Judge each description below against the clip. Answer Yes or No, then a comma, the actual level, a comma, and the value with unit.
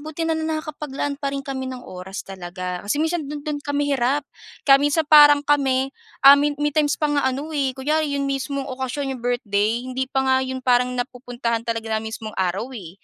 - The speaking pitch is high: Yes, very high, 270 Hz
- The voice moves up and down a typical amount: Yes, average, 3.0 semitones